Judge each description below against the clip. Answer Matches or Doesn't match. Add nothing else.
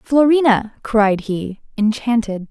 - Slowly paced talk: Matches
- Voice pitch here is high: Matches